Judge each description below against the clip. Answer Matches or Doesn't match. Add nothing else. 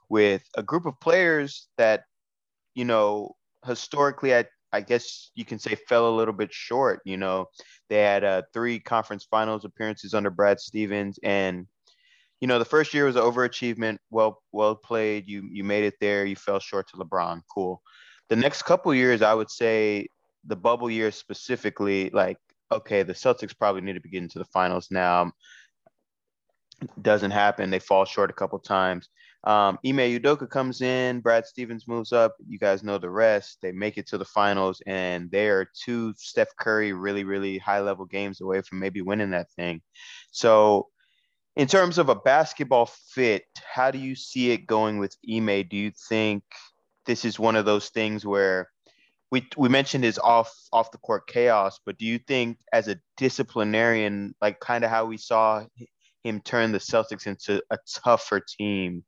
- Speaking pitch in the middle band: Doesn't match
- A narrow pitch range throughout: Doesn't match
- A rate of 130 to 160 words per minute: Doesn't match